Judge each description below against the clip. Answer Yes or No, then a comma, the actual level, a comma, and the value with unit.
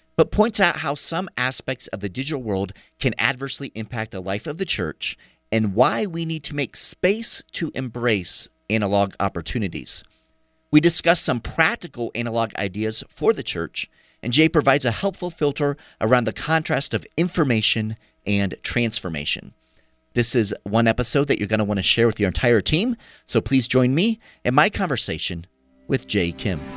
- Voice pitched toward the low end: Yes, low, 125 Hz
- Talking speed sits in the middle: Yes, average, 170 wpm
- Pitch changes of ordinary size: No, wide, 6.9 semitones